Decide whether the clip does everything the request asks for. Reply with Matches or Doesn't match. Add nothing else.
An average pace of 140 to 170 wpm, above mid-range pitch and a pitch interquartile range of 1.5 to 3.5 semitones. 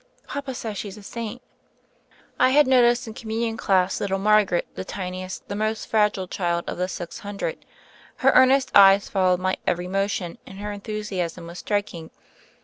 Matches